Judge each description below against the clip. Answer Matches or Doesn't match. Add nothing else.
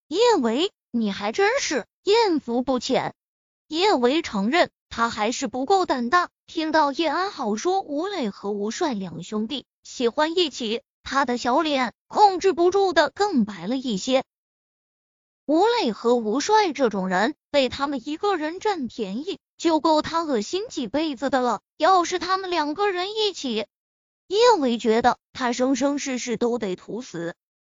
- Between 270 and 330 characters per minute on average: Doesn't match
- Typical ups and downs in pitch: Doesn't match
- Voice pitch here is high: Matches